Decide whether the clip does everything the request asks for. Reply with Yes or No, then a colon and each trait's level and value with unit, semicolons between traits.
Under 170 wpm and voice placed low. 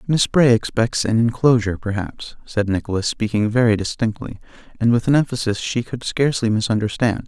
Yes: average, 155 wpm; low, 115 Hz